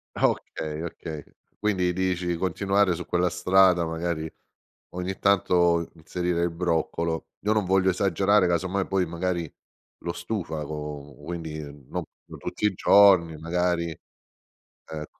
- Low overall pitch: Yes, very low, 85 Hz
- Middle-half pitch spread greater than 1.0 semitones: Yes, narrow, 2.4 semitones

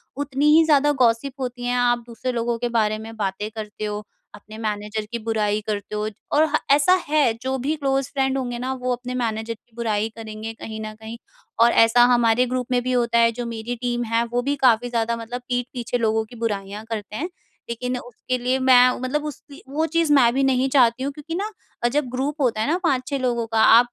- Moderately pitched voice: No, high, 240 Hz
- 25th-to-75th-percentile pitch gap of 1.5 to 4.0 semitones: Yes, average, 2.8 semitones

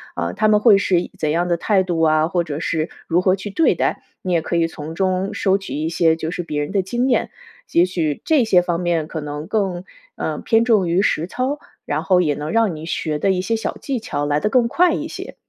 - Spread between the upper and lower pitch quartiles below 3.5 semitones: No, average, 4.0 semitones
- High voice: No, medium, 180 Hz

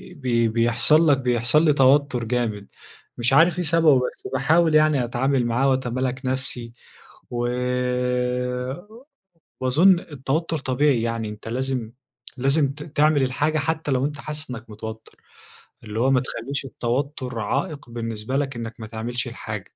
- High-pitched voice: No, low, 130 Hz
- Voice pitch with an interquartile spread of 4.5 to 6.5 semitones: No, average, 3.7 semitones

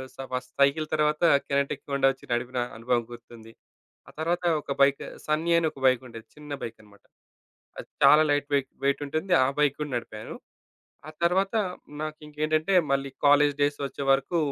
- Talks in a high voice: No, medium, 140 Hz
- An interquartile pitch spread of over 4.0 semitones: No, average, 3.2 semitones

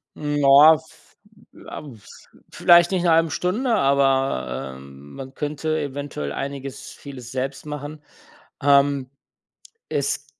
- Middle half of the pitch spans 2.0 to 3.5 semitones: Yes, narrow, 2.5 semitones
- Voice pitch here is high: No, medium, 140 Hz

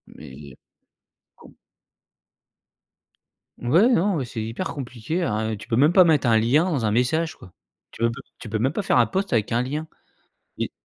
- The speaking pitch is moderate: No, low, 125 Hz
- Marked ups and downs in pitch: Yes, wide, 6.2 semitones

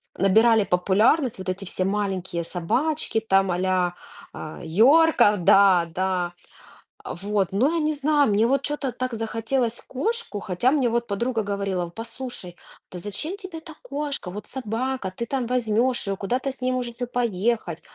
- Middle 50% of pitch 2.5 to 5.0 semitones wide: No, wide, 5.4 semitones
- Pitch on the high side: Yes, high, 225 Hz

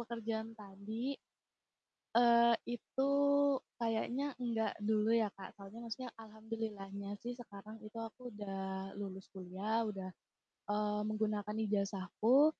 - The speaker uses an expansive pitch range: No, narrow, 2.5 semitones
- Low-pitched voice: No, high, 215 Hz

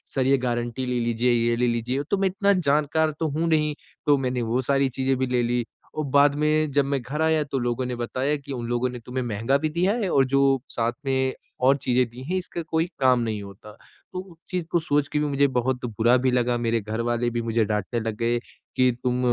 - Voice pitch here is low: Yes, low, 130 Hz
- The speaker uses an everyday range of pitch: Yes, average, 3.4 semitones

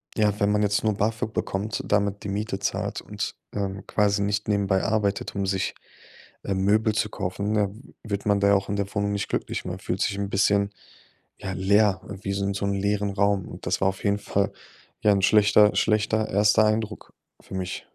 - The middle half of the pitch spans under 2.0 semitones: Yes, narrow, 1.2 semitones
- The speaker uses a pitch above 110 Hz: No, low, 100 Hz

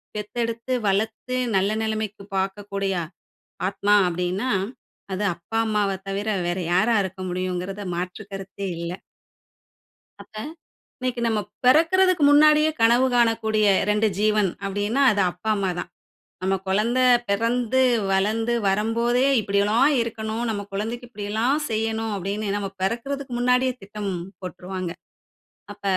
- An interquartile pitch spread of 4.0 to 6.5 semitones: No, average, 3.3 semitones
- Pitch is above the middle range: Yes, high, 215 Hz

